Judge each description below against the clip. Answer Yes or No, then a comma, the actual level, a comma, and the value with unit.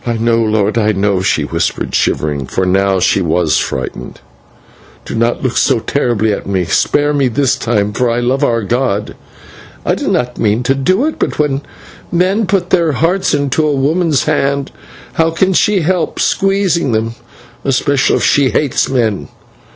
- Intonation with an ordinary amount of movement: No, wide, 6.1 semitones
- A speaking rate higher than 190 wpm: No, average, 175 wpm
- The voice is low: Yes, low, 130 Hz